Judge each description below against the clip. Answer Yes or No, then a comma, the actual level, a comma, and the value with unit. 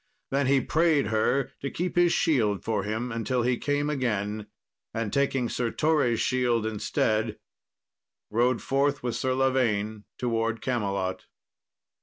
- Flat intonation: No, average, 3.9 semitones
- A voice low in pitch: Yes, low, 120 Hz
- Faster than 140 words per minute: No, slow, 135 wpm